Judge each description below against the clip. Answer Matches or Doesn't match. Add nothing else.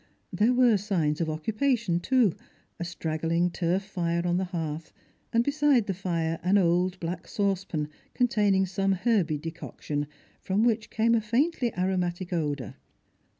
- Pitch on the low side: Doesn't match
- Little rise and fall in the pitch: Doesn't match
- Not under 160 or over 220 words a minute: Doesn't match